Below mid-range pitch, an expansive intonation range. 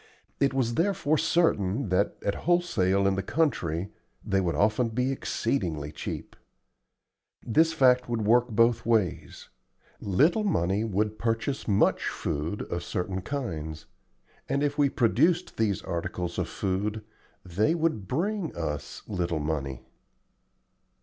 Yes: low, 110 Hz; wide, 7.2 semitones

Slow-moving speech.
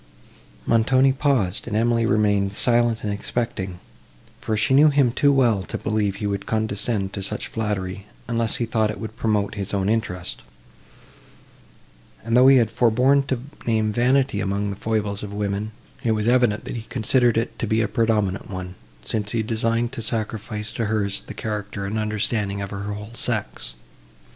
No: average, 175 wpm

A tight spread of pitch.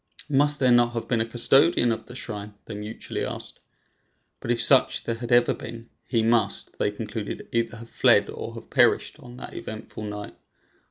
Yes: narrow, 1.9 semitones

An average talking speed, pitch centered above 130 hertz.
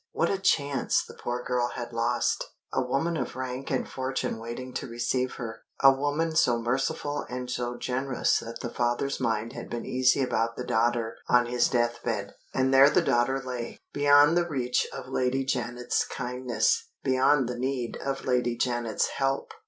No: average, 175 wpm; low, 125 Hz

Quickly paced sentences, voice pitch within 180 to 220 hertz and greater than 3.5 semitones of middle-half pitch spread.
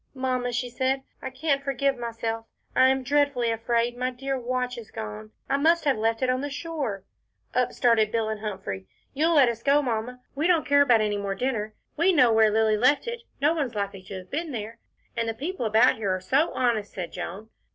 No: fast, 215 wpm; high, 245 Hz; average, 4.0 semitones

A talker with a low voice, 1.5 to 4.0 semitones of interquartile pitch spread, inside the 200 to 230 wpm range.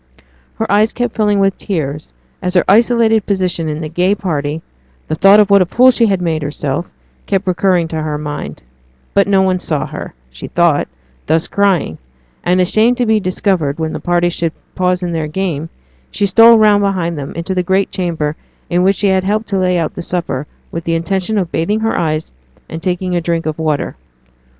No: medium, 180 Hz; average, 3.6 semitones; fast, 205 wpm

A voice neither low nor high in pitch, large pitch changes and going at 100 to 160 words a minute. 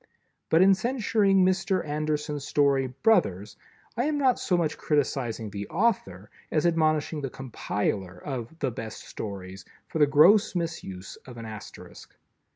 Yes: medium, 150 Hz; wide, 8.4 semitones; average, 145 wpm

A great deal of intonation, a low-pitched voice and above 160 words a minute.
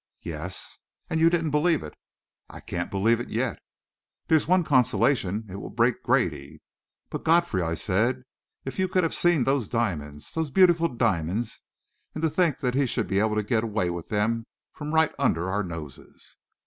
Yes: wide, 8.6 semitones; low, 115 Hz; average, 175 wpm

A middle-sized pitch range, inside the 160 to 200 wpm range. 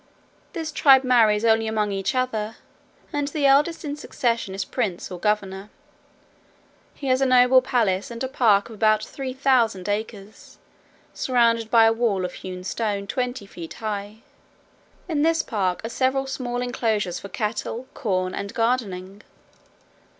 No: average, 4.1 semitones; average, 150 wpm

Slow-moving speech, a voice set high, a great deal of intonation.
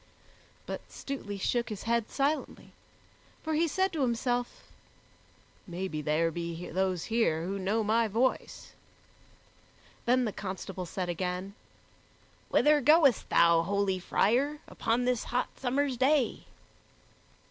Yes: slow, 120 wpm; high, 225 Hz; wide, 5.7 semitones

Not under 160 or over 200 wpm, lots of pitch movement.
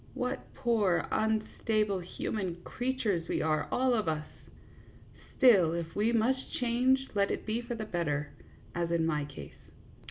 No: average, 150 wpm; wide, 5.9 semitones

